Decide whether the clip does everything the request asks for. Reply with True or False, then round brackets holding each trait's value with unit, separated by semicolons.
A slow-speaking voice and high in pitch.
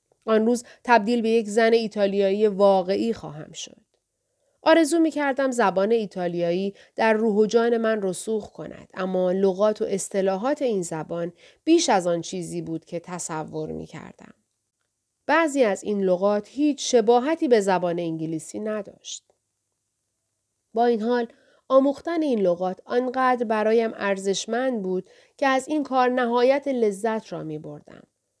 False (140 wpm; 215 Hz)